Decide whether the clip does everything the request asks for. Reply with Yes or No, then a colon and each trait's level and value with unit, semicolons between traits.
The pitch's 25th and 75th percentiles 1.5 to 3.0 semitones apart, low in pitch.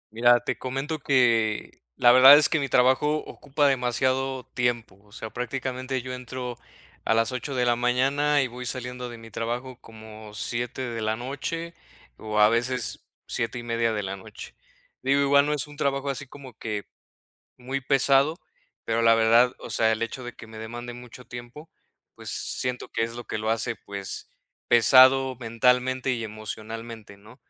Yes: narrow, 2.5 semitones; low, 125 Hz